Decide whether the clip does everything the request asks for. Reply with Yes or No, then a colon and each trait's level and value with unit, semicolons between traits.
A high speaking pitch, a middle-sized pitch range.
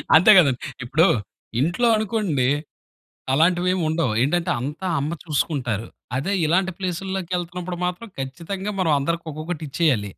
No: medium, 170 Hz; average, 4.4 semitones